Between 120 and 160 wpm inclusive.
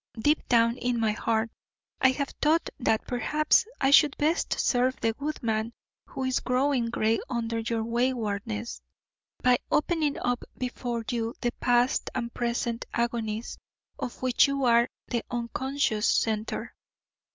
Yes: average, 140 wpm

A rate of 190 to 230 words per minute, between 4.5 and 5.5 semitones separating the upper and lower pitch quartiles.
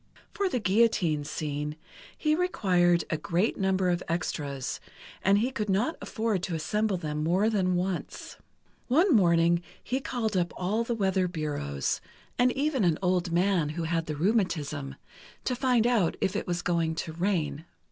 No: average, 165 wpm; average, 5.0 semitones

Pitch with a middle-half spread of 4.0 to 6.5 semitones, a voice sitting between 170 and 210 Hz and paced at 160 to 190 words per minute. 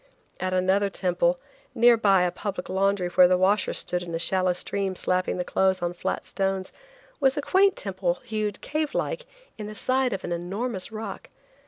No: average, 2.9 semitones; high, 190 Hz; average, 185 wpm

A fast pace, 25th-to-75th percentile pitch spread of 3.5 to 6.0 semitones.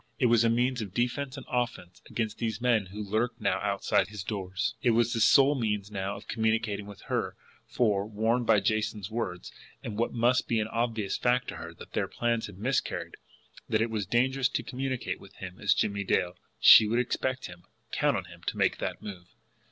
No: fast, 210 wpm; average, 3.0 semitones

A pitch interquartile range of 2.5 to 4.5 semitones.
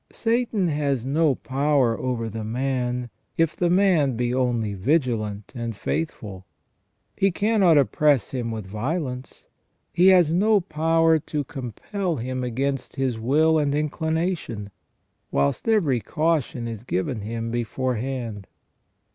No: wide, 5.6 semitones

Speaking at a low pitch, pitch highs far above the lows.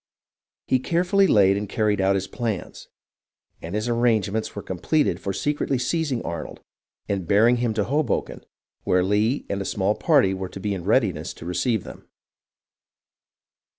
No: low, 105 Hz; average, 4.2 semitones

